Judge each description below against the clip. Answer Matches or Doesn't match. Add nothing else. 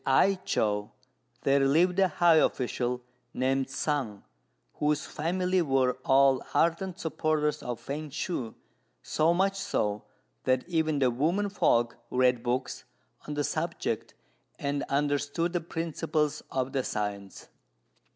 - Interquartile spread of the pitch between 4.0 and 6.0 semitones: Matches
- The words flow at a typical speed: Doesn't match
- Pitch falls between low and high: Matches